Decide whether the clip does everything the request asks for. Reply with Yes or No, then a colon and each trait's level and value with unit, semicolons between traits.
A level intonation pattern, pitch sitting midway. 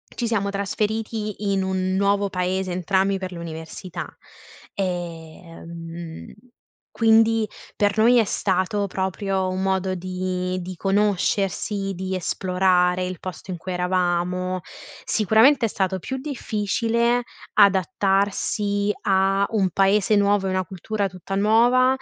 No: narrow, 2.2 semitones; high, 195 Hz